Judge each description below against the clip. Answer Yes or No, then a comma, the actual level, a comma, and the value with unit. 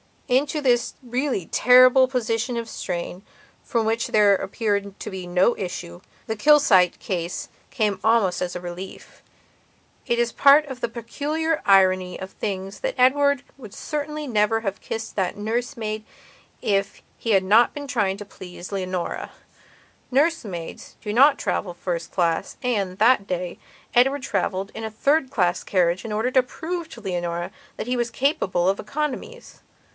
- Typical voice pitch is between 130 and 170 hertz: No, high, 220 Hz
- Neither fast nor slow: Yes, average, 160 wpm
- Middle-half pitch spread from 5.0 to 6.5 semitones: Yes, average, 5.3 semitones